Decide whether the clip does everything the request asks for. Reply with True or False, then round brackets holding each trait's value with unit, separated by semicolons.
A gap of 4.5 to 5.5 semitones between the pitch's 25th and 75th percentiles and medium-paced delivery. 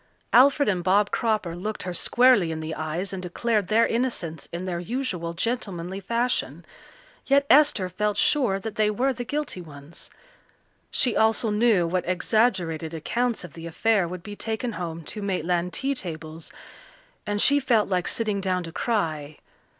True (5.2 semitones; 165 wpm)